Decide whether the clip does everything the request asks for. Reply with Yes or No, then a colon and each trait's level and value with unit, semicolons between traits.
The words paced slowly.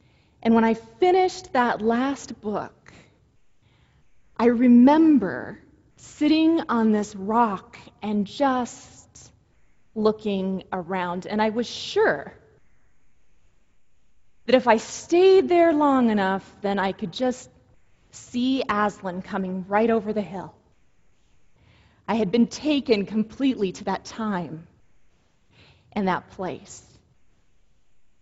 Yes: slow, 105 wpm